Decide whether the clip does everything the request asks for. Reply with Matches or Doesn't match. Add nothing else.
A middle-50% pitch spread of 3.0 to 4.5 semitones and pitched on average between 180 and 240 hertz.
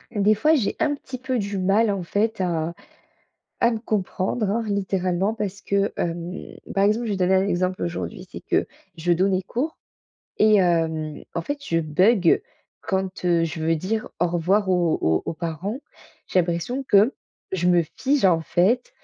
Matches